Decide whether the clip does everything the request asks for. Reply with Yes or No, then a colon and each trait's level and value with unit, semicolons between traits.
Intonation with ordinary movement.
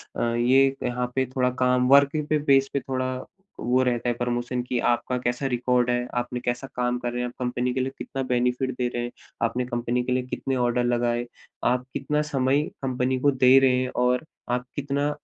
No: narrow, 1.3 semitones